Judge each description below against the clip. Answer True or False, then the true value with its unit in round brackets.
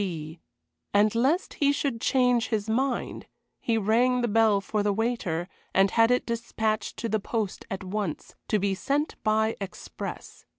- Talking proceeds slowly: False (165 wpm)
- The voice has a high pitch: True (220 Hz)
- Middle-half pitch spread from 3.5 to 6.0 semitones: False (3.1 semitones)